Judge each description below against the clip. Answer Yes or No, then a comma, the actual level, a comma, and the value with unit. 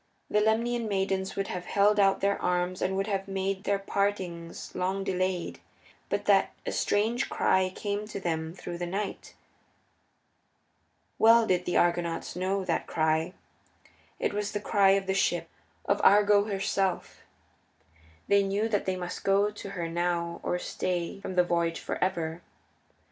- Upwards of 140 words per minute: Yes, average, 160 wpm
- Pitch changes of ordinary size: No, narrow, 2.3 semitones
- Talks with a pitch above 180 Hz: Yes, high, 190 Hz